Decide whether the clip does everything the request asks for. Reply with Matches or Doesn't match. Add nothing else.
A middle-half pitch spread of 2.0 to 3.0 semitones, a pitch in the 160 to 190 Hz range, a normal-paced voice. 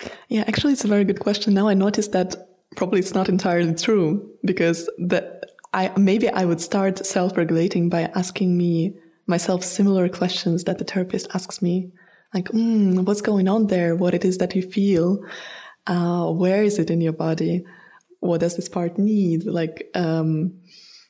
Matches